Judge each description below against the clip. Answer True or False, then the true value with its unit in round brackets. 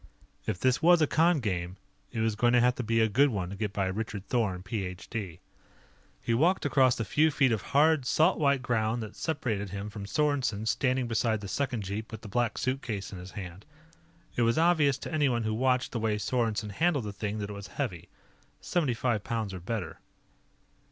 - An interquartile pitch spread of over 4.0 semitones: True (4.4 semitones)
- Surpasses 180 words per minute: True (205 wpm)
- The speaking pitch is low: True (115 Hz)